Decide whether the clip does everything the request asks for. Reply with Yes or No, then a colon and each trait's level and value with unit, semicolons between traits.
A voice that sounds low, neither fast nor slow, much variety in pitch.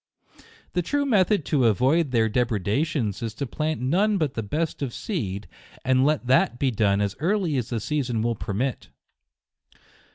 Yes: low, 130 Hz; average, 170 wpm; wide, 5.8 semitones